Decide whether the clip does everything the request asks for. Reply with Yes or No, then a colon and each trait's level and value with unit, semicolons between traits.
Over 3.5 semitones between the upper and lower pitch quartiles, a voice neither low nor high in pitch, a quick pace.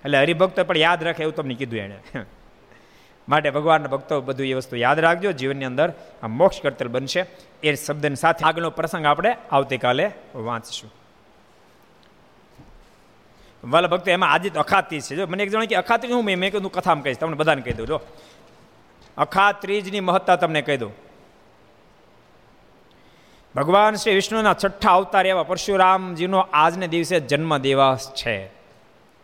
Yes: wide, 5.4 semitones; medium, 155 Hz; fast, 145 wpm